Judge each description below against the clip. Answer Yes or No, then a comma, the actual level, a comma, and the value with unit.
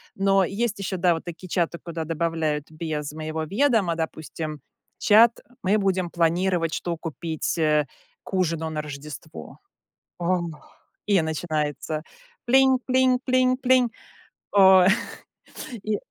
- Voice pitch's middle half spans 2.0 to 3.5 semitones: No, average, 4.1 semitones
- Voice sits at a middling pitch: Yes, medium, 170 Hz